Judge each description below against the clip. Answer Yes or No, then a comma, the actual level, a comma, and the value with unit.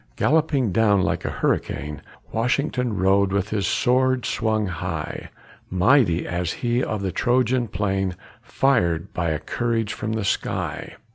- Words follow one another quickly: No, average, 140 wpm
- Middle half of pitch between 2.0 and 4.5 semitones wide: No, average, 4.9 semitones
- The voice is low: Yes, low, 110 Hz